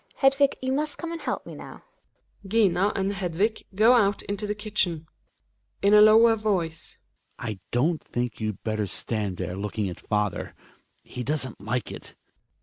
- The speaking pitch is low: No, medium, 185 Hz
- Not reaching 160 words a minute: No, average, 165 wpm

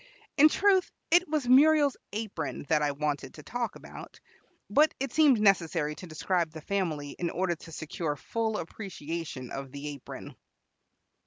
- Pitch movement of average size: No, wide, 8.4 semitones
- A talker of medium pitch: Yes, medium, 175 Hz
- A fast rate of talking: No, average, 155 wpm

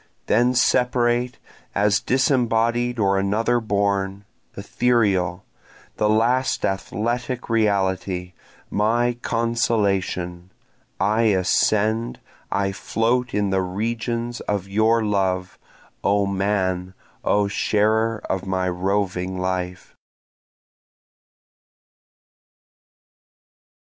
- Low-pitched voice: Yes, low, 105 Hz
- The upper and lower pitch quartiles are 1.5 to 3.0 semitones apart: No, average, 3.4 semitones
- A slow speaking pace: Yes, slow, 80 wpm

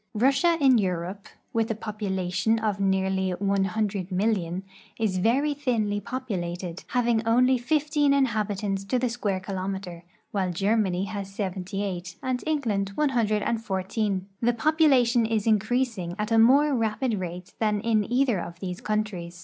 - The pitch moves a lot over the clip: No, average, 3.9 semitones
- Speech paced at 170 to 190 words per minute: No, average, 145 wpm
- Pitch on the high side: Yes, high, 210 Hz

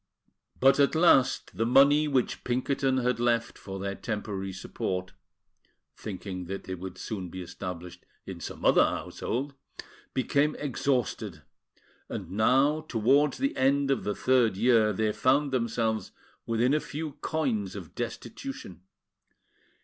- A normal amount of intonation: No, wide, 5.8 semitones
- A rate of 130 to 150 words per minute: Yes, slow, 135 wpm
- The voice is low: Yes, low, 120 Hz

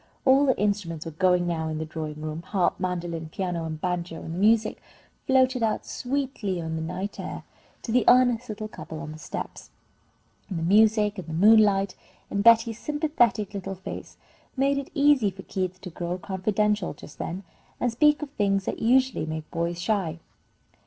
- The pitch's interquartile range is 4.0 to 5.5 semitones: Yes, average, 5.2 semitones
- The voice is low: No, high, 195 Hz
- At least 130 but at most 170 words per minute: No, average, 180 wpm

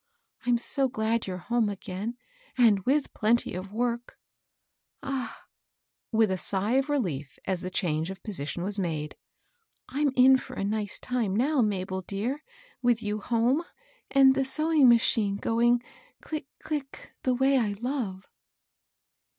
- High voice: Yes, high, 230 Hz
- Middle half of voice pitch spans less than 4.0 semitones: No, average, 5.0 semitones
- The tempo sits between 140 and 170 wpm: Yes, average, 160 wpm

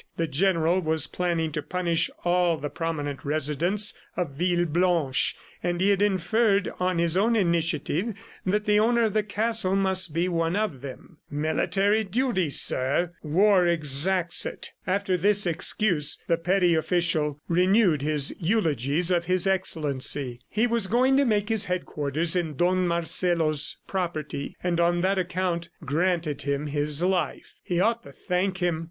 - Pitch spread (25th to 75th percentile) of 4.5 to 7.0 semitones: No, average, 3.6 semitones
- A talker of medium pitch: Yes, medium, 175 Hz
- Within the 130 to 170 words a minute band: Yes, average, 150 wpm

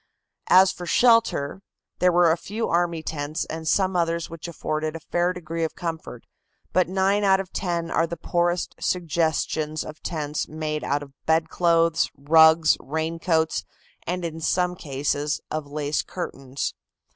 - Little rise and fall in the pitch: Yes, narrow, 2.3 semitones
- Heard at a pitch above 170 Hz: No, medium, 165 Hz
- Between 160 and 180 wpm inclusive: No, average, 150 wpm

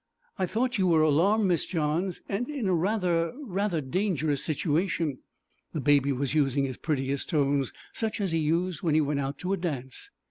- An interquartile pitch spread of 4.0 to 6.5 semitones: Yes, average, 4.8 semitones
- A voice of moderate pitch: Yes, medium, 165 Hz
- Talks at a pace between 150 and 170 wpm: No, average, 185 wpm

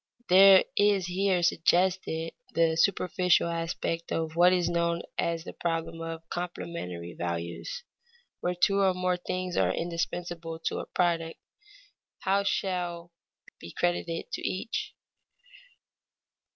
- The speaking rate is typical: No, slow, 125 wpm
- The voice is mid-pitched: Yes, medium, 175 Hz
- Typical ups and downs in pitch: No, narrow, 1.8 semitones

